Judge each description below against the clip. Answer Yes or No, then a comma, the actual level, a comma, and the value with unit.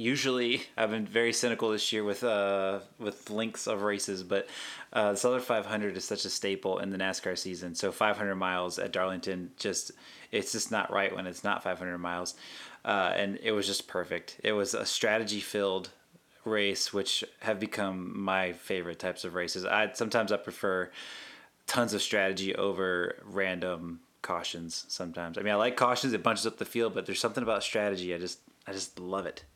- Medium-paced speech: Yes, average, 195 wpm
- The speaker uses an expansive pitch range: No, average, 2.7 semitones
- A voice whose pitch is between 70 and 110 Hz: Yes, low, 100 Hz